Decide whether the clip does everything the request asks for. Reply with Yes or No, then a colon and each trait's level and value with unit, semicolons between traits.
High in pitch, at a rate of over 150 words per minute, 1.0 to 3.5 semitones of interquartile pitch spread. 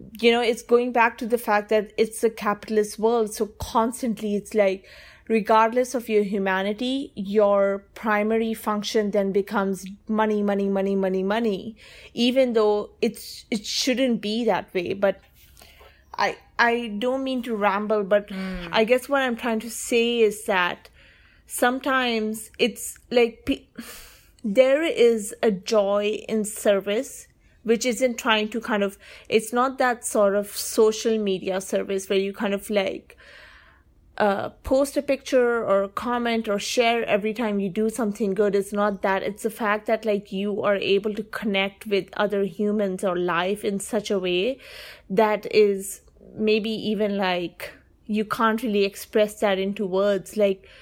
Yes: high, 215 Hz; average, 160 wpm; narrow, 2.5 semitones